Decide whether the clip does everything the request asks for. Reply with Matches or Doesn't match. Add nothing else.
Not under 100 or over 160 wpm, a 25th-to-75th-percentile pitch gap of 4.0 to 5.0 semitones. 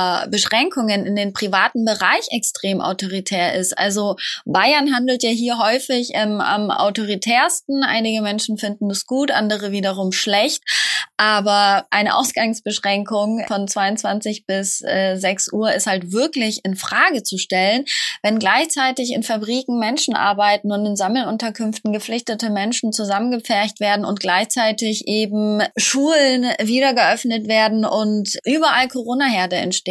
Doesn't match